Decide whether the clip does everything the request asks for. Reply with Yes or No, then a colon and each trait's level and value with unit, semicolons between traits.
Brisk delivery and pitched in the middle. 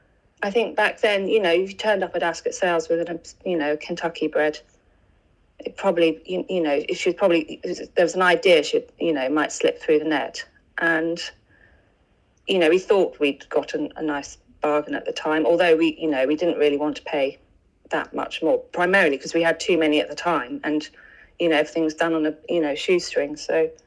Yes: fast, 220 wpm; medium, 165 Hz